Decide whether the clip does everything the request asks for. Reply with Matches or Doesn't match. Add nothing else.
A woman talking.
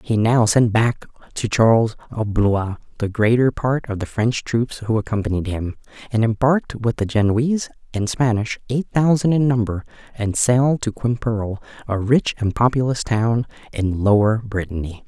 Doesn't match